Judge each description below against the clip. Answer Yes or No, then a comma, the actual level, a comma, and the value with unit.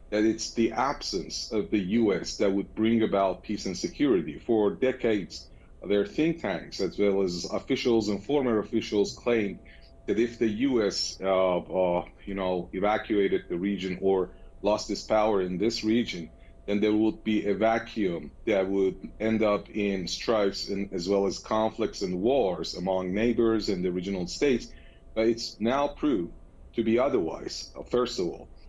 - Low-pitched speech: Yes, low, 100 Hz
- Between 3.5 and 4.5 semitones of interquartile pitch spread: No, average, 3.0 semitones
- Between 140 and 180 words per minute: Yes, average, 165 wpm